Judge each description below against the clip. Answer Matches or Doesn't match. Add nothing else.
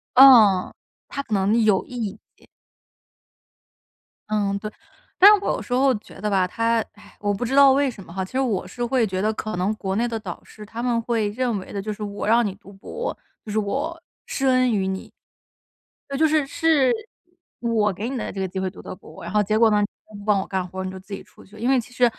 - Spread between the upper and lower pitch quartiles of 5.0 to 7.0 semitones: Doesn't match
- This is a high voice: Matches